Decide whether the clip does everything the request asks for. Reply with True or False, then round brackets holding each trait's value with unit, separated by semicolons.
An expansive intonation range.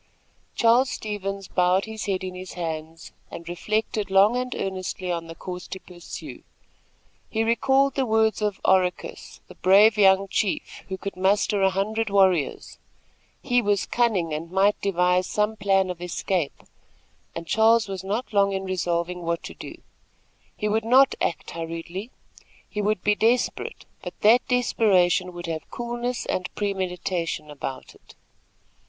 False (3.4 semitones)